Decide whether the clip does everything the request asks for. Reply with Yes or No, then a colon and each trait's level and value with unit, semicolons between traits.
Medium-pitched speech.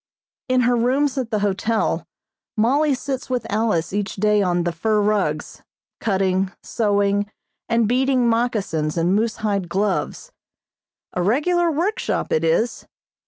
No: high, 215 Hz